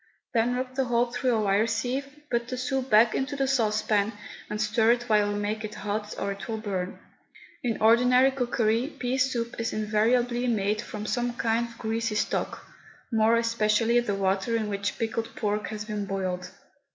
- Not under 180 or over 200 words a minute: Yes, average, 185 wpm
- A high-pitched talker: Yes, high, 225 Hz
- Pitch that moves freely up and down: No, narrow, 2.4 semitones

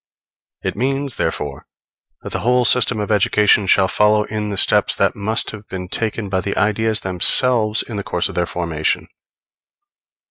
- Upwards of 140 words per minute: Yes, average, 170 wpm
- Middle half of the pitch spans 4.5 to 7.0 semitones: No, average, 2.8 semitones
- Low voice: Yes, low, 105 Hz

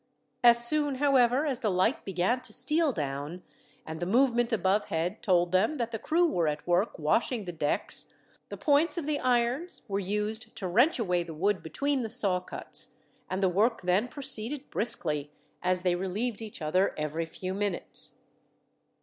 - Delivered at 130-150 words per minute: No, average, 175 wpm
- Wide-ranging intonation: Yes, wide, 5.8 semitones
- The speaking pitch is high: Yes, high, 210 Hz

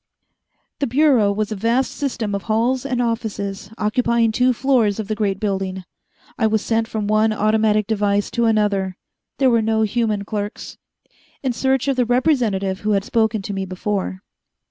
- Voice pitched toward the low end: No, high, 220 Hz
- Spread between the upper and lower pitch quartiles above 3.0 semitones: No, average, 2.7 semitones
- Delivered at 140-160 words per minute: No, average, 170 wpm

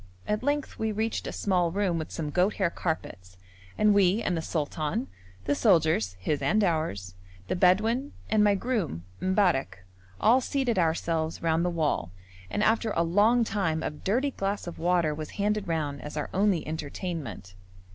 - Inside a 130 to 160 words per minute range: No, average, 170 wpm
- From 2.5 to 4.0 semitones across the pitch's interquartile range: No, average, 5.1 semitones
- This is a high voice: No, medium, 180 Hz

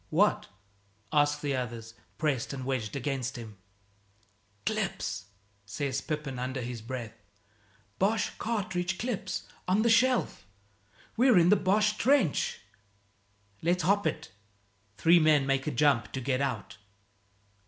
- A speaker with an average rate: No, slow, 125 wpm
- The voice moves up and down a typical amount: No, wide, 6.9 semitones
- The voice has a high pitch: No, medium, 145 Hz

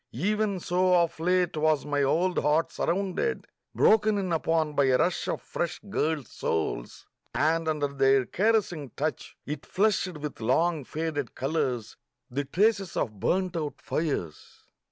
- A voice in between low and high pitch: Yes, medium, 160 Hz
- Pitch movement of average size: Yes, average, 4.3 semitones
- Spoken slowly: No, average, 145 wpm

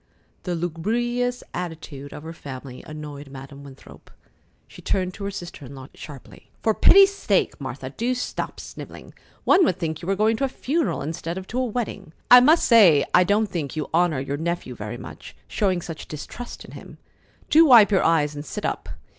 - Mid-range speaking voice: Yes, medium, 175 Hz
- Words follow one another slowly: No, average, 195 wpm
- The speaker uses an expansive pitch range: Yes, wide, 7.2 semitones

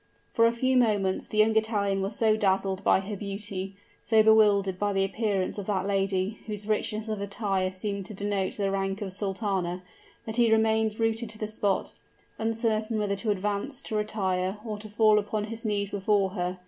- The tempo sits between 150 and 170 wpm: No, average, 190 wpm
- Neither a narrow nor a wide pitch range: No, narrow, 2.0 semitones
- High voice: Yes, high, 205 Hz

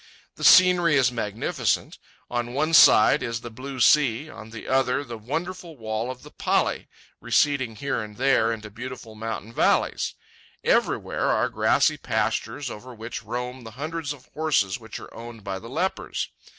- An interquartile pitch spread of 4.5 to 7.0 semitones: No, average, 4.1 semitones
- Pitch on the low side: Yes, low, 125 Hz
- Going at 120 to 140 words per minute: No, average, 165 wpm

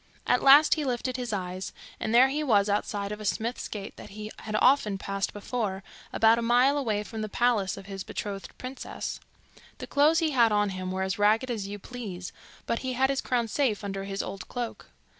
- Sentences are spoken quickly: Yes, fast, 210 wpm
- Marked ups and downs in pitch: No, average, 3.9 semitones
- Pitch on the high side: Yes, high, 220 Hz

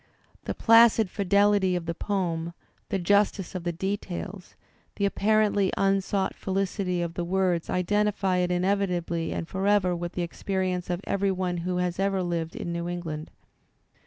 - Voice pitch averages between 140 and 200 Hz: Yes, medium, 185 Hz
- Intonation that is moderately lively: No, narrow, 2.3 semitones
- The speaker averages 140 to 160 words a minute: Yes, average, 150 wpm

